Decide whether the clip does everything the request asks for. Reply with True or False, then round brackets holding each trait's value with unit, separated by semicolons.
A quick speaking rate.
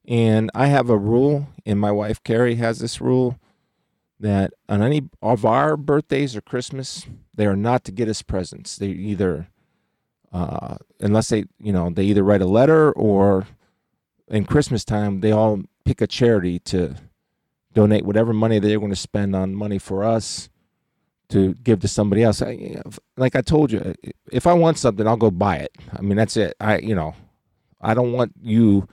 False (185 wpm)